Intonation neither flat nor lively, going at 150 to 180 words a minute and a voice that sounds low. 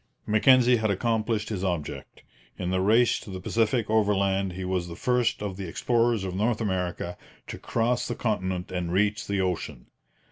Yes: average, 3.6 semitones; average, 175 wpm; low, 100 Hz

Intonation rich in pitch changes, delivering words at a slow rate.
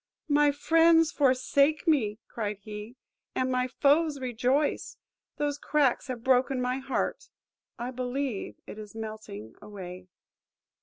No: average, 4.7 semitones; slow, 120 wpm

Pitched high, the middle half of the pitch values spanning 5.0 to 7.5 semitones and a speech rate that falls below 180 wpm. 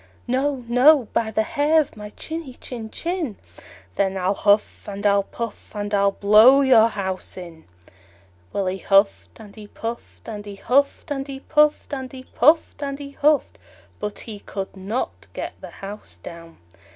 Yes: high, 220 Hz; wide, 5.5 semitones; average, 170 wpm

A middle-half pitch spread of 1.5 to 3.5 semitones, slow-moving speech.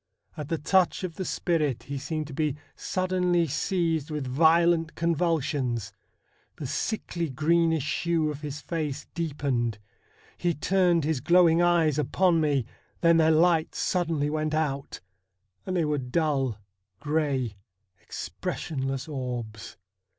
Yes: average, 3.2 semitones; slow, 130 wpm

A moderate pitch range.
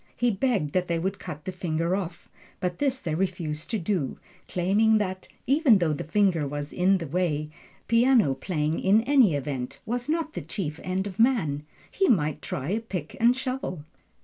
No: wide, 6.4 semitones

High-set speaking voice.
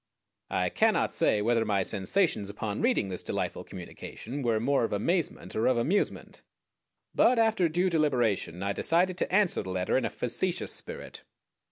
No: low, 125 Hz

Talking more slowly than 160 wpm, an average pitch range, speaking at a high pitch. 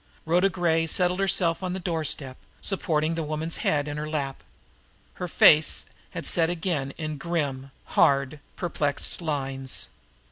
No: average, 140 wpm; average, 3.1 semitones; medium, 155 Hz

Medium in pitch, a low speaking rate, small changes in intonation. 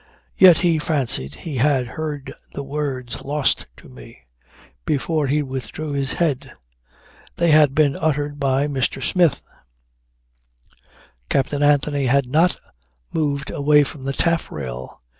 Yes: medium, 145 Hz; slow, 125 wpm; narrow, 2.3 semitones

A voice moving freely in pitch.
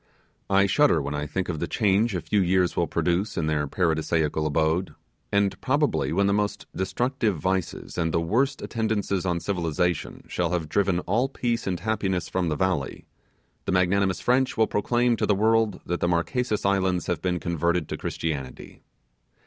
No: average, 3.6 semitones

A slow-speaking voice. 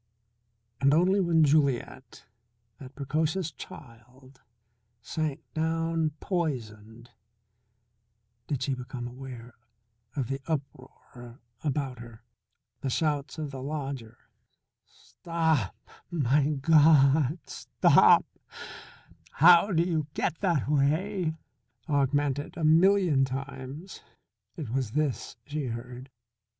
Yes: slow, 95 wpm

